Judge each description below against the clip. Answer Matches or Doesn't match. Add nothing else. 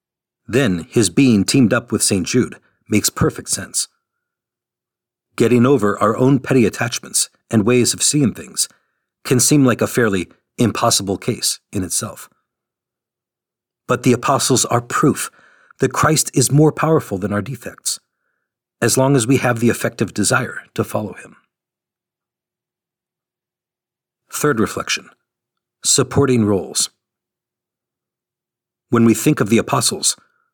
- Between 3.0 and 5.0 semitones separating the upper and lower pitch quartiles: Matches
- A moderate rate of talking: Doesn't match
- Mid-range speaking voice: Doesn't match